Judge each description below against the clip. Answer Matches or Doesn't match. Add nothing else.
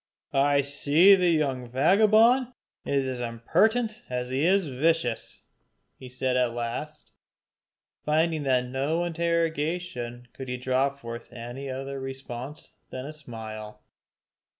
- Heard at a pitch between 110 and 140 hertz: Matches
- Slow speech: Matches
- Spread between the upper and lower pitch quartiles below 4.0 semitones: Doesn't match